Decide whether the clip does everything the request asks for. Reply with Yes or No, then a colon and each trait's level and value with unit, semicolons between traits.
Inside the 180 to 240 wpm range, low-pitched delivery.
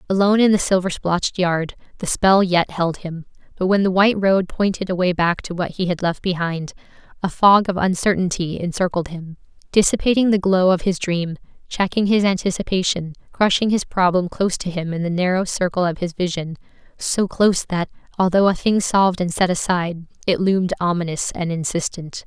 No: average, 185 wpm; medium, 180 Hz